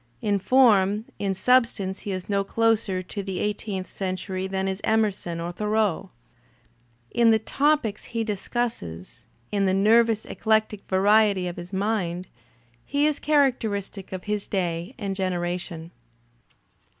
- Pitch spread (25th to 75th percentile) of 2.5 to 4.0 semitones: Yes, average, 2.9 semitones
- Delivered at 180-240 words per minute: No, average, 140 wpm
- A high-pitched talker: Yes, high, 200 Hz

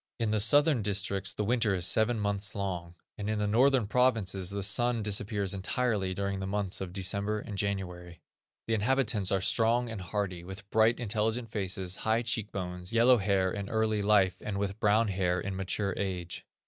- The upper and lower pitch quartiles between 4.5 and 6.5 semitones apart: No, narrow, 2.6 semitones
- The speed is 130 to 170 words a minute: No, average, 185 wpm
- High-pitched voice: No, low, 100 Hz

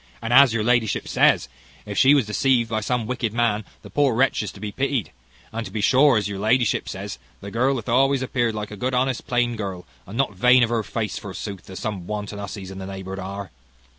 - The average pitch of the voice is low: Yes, low, 110 Hz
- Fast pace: Yes, fast, 230 wpm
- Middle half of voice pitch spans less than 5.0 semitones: Yes, average, 3.7 semitones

